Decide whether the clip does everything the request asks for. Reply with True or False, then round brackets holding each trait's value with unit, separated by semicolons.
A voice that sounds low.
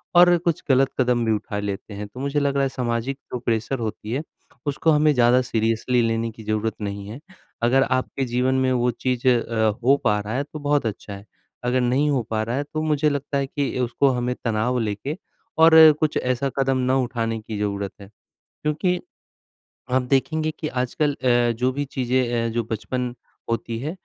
True (125 Hz)